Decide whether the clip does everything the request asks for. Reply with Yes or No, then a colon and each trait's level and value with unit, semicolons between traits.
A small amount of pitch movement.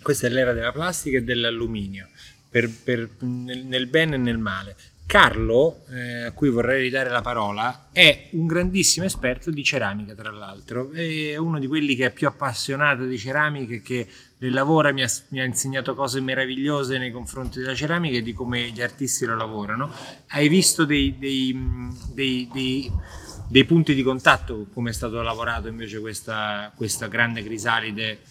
No: average, 3.0 semitones